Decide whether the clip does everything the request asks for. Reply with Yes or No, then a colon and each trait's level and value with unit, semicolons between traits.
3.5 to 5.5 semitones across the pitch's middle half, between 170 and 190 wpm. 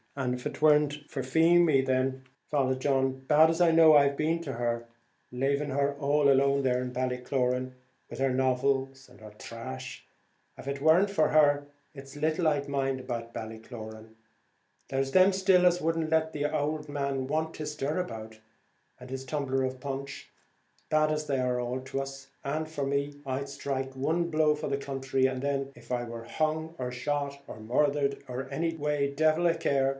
No: average, 2.7 semitones; average, 180 wpm